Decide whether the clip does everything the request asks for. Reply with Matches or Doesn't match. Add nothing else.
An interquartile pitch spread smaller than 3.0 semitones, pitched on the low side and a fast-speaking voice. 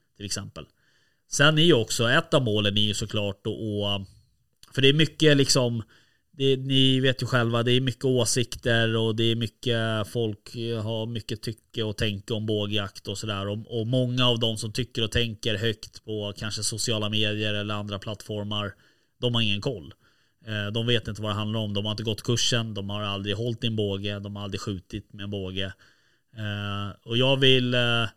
Matches